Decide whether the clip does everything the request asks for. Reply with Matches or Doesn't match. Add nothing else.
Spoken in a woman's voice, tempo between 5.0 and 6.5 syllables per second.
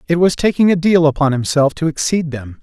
Doesn't match